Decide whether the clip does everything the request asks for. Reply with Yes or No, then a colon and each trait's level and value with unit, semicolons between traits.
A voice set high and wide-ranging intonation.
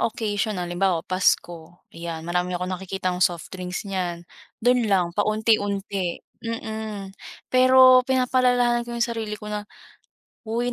No: high, 205 Hz; average, 4.2 semitones